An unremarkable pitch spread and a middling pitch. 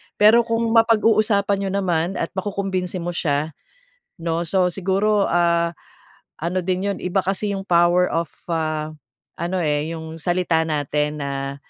Yes: average, 3.4 semitones; medium, 180 Hz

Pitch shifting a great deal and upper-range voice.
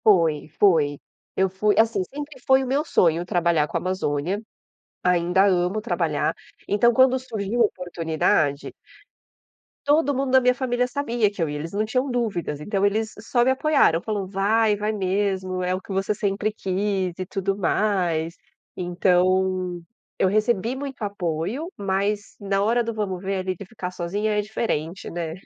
No: average, 3.7 semitones; high, 195 Hz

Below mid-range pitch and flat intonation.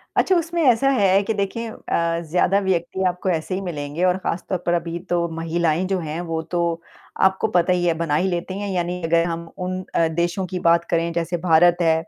No: medium, 175 Hz; narrow, 2.1 semitones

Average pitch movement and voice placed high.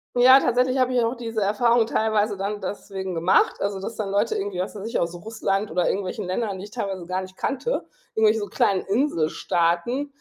Yes: average, 3.6 semitones; high, 205 Hz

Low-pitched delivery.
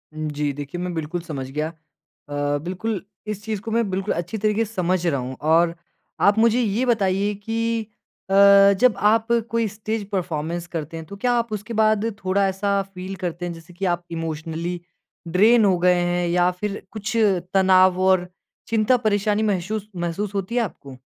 No: high, 190 Hz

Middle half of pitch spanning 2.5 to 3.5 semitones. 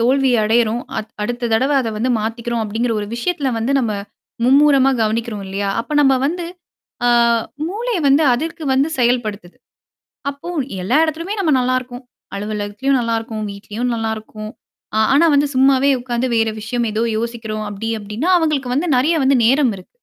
No: average, 3.9 semitones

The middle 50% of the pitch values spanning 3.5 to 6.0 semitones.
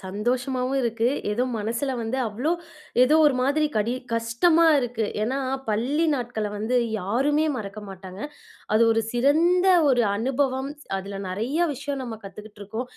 Yes: average, 4.1 semitones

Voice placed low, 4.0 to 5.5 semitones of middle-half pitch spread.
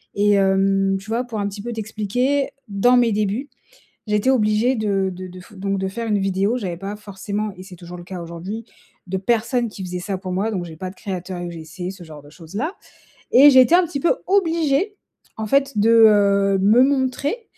No: high, 205 Hz; average, 4.3 semitones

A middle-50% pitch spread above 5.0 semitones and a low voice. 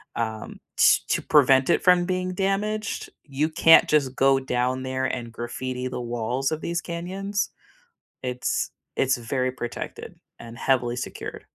Yes: wide, 5.4 semitones; low, 130 Hz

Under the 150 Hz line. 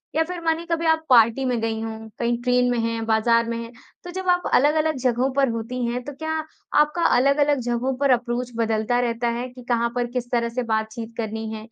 No: high, 245 Hz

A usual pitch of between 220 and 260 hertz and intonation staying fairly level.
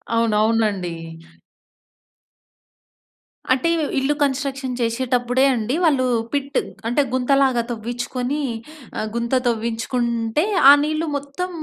No: very high, 250 Hz; average, 3.2 semitones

